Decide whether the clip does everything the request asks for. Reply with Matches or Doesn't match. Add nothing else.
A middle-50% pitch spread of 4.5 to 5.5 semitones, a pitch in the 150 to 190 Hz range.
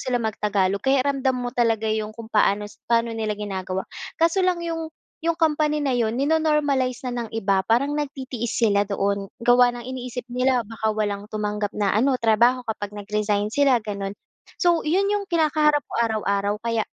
Doesn't match